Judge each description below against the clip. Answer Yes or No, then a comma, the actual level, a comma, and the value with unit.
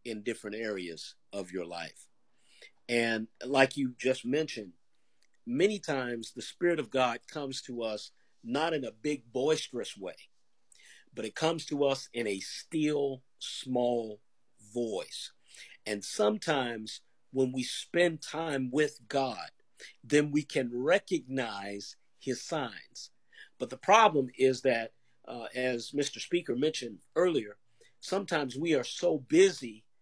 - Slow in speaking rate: Yes, slow, 130 wpm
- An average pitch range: Yes, average, 4.5 semitones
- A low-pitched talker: Yes, low, 130 Hz